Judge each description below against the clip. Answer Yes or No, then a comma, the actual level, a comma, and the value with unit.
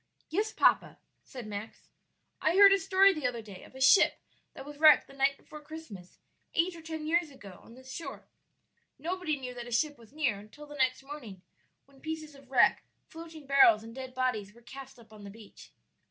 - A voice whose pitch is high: Yes, very high, 270 Hz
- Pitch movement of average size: Yes, average, 5.0 semitones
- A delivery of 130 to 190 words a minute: No, fast, 205 wpm